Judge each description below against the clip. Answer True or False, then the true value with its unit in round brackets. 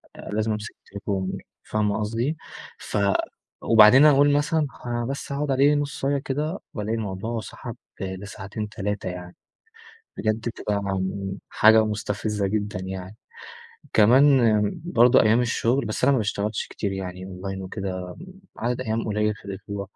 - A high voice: False (105 Hz)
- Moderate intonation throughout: True (3.5 semitones)